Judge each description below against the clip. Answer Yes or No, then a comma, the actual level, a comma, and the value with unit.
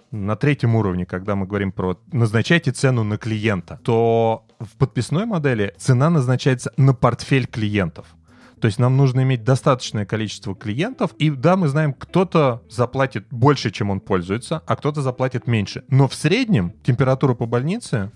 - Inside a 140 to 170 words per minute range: Yes, fast, 160 wpm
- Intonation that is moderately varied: Yes, average, 4.5 semitones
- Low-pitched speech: Yes, low, 125 Hz